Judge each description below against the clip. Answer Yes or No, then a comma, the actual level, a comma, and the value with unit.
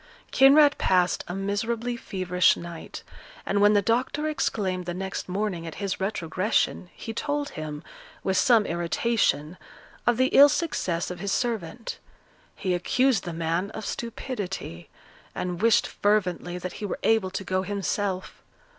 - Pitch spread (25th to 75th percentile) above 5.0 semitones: No, average, 4.3 semitones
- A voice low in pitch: No, high, 195 Hz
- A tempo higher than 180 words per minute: No, average, 145 wpm